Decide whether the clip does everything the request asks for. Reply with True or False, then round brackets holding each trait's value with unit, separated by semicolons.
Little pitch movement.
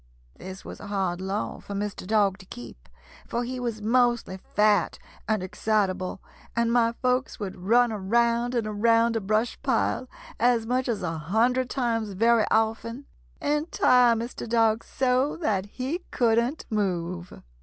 False (3.4 semitones)